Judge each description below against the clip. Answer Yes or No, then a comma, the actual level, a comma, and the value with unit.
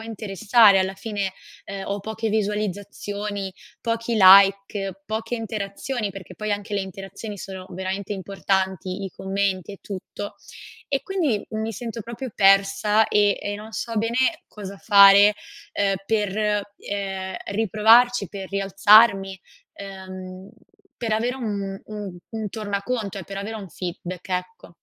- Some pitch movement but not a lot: No, narrow, 2.0 semitones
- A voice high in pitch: Yes, high, 200 Hz